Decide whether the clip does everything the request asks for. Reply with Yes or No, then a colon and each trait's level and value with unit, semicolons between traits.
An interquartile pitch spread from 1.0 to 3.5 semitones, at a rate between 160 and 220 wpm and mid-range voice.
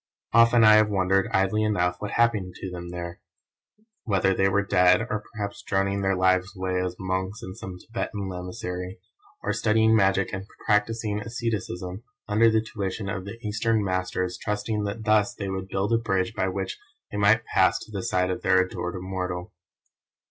No: narrow, 2.6 semitones; average, 175 wpm; very low, 95 Hz